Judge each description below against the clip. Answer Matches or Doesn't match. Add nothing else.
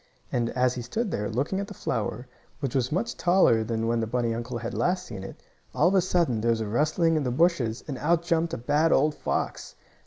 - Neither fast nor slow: Doesn't match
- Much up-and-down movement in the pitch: Matches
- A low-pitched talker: Matches